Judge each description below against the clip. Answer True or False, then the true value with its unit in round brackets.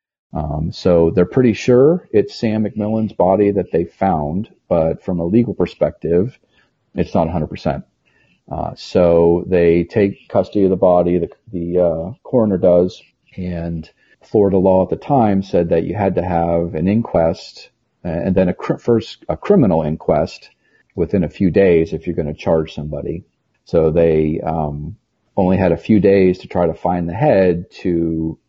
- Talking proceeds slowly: False (170 wpm)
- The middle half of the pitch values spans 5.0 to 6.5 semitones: False (3.1 semitones)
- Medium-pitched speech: False (90 Hz)